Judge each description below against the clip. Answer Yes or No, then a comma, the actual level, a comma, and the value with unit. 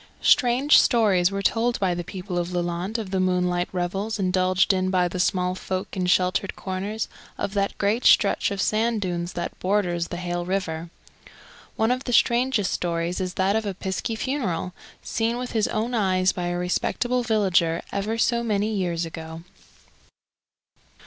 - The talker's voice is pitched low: No, high, 190 Hz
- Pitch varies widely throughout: No, average, 3.5 semitones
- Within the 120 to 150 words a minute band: No, average, 170 wpm